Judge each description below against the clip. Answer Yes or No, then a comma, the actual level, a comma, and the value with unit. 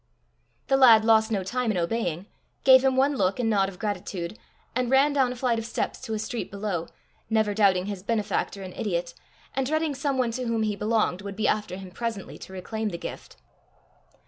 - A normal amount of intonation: Yes, average, 4.4 semitones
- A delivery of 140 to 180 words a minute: No, fast, 205 wpm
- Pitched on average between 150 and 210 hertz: No, high, 220 Hz